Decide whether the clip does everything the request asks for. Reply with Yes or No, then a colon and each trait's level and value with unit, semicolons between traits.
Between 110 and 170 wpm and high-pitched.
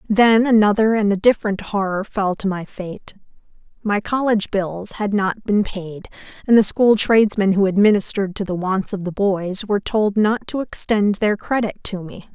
No: average, 185 wpm; high, 205 Hz